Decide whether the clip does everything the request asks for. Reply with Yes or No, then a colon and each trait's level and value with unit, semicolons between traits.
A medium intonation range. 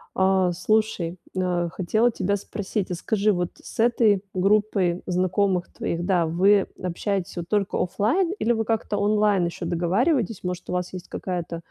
Yes: average, 3.0 semitones